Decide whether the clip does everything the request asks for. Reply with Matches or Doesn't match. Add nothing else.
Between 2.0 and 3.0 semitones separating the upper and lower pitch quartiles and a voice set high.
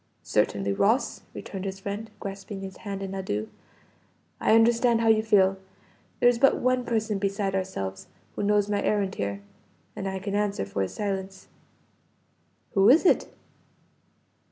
Matches